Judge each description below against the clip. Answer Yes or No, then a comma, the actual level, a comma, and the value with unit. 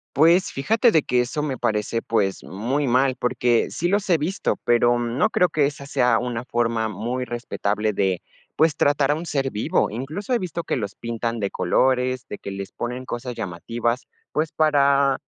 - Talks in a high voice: No, low, 125 Hz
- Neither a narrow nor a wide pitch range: Yes, average, 4.2 semitones